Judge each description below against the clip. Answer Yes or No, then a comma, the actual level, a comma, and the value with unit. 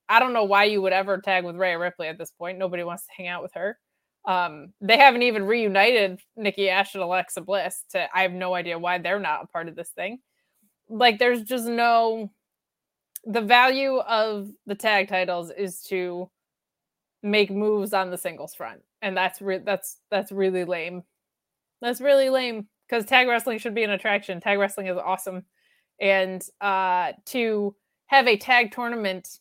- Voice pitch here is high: Yes, high, 200 Hz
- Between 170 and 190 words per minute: Yes, average, 185 wpm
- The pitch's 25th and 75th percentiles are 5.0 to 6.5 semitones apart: No, average, 3.5 semitones